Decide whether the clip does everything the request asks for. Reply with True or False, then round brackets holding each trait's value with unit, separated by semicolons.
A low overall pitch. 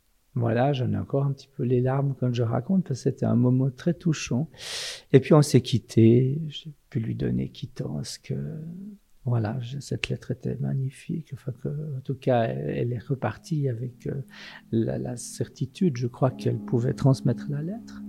True (130 Hz)